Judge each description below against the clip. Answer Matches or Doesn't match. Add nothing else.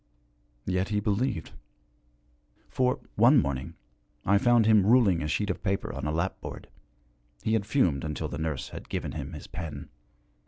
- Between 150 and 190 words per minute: Matches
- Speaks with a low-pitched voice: Matches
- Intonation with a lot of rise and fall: Matches